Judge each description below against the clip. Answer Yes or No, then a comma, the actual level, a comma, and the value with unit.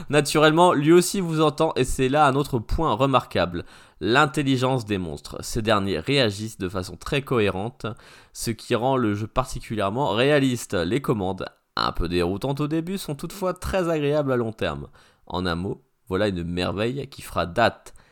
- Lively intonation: Yes, wide, 7.1 semitones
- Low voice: Yes, low, 130 Hz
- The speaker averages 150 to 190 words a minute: Yes, average, 170 wpm